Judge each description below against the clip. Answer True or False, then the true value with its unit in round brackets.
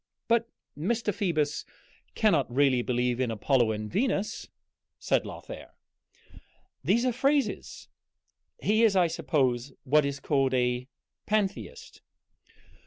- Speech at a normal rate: False (110 wpm)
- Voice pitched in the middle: True (150 Hz)